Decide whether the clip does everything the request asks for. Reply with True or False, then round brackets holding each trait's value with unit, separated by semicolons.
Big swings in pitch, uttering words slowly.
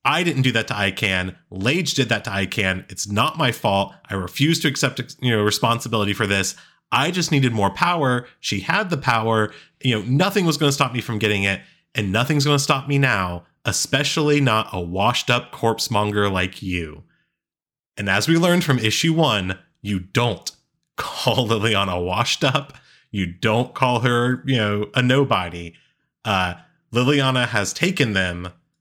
False (6.0 semitones; 175 wpm)